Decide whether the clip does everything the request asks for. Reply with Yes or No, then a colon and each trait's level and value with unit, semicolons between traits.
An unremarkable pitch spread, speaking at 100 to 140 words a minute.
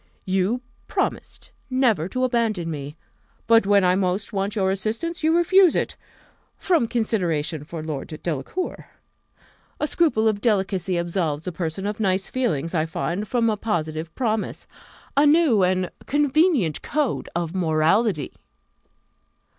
No: wide, 6.2 semitones; slow, 135 wpm